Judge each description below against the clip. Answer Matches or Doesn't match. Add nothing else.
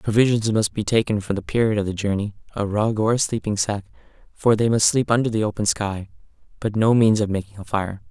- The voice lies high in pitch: Doesn't match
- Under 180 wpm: Doesn't match